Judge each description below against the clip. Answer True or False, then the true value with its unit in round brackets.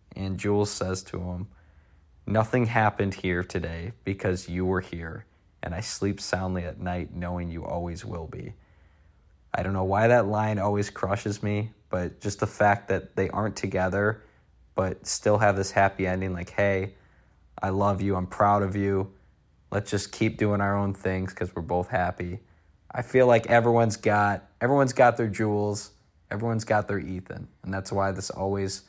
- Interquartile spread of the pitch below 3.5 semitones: True (2.5 semitones)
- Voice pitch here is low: True (95 Hz)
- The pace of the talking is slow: False (175 wpm)